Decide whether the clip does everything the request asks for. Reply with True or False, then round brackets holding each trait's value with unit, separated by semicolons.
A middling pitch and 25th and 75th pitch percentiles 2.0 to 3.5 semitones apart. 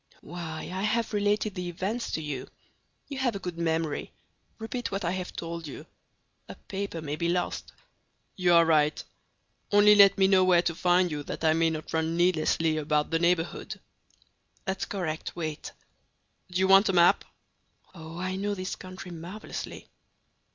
True (175 Hz; 3.1 semitones)